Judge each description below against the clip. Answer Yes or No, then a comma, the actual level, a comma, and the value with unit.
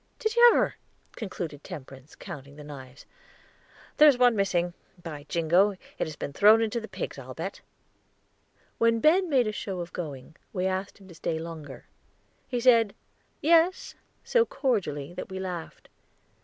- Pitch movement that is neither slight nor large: No, wide, 6.9 semitones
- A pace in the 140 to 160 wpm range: Yes, average, 155 wpm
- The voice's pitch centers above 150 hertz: Yes, high, 190 Hz